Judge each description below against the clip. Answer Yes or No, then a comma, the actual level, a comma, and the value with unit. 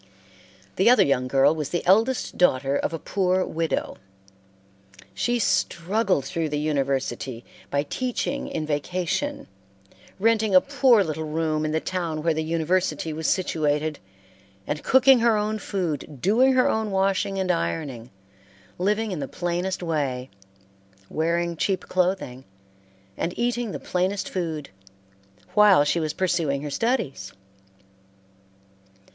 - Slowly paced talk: Yes, slow, 130 wpm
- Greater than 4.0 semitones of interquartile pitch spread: Yes, average, 5.0 semitones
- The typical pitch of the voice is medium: Yes, medium, 170 Hz